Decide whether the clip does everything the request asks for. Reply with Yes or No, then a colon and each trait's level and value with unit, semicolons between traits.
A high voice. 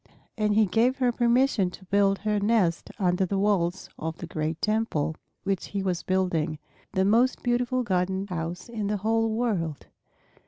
Yes: high, 200 Hz